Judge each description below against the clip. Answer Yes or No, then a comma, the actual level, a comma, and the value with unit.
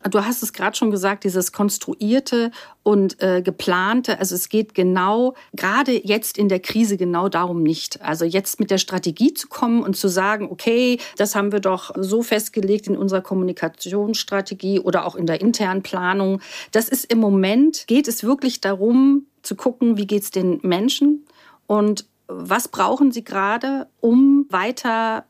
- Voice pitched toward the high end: Yes, high, 210 Hz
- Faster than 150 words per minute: Yes, average, 170 wpm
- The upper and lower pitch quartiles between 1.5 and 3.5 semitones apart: No, average, 3.9 semitones